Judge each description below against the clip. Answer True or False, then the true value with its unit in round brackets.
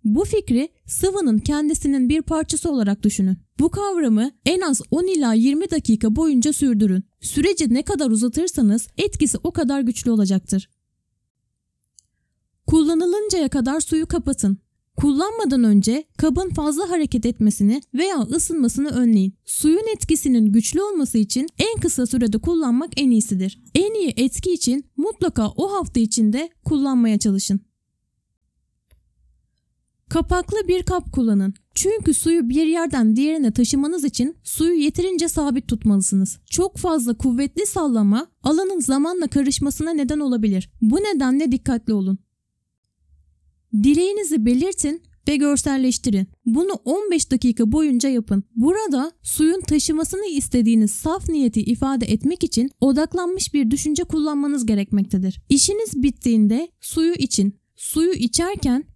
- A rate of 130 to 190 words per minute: False (120 wpm)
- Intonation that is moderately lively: False (5.9 semitones)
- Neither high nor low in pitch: False (275 Hz)